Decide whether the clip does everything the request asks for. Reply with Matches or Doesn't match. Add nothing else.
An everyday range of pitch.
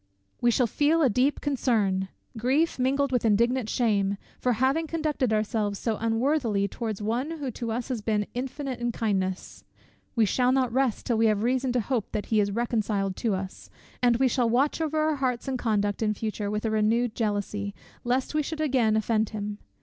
Matches